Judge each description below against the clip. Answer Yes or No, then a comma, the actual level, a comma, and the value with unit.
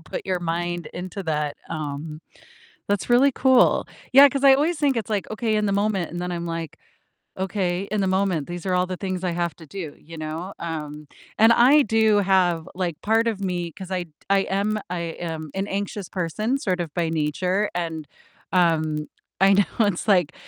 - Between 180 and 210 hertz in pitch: Yes, medium, 185 Hz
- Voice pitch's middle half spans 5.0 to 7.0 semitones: No, average, 3.7 semitones